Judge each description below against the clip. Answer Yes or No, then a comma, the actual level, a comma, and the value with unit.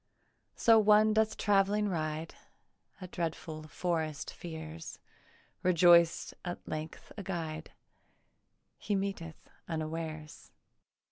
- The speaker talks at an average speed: No, slow, 90 wpm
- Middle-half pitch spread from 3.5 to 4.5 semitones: Yes, average, 3.8 semitones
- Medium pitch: Yes, medium, 170 Hz